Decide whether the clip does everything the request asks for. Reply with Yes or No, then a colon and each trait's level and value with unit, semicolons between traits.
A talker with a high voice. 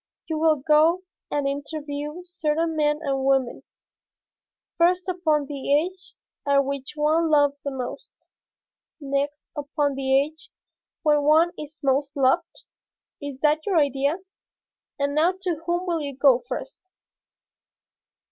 Yes: very high, 295 Hz